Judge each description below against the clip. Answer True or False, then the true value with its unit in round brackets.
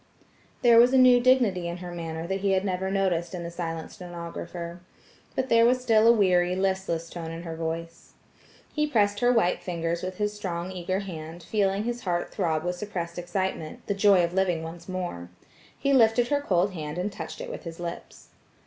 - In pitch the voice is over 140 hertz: True (185 Hz)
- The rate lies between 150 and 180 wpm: False (195 wpm)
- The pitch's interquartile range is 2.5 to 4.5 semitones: True (3.5 semitones)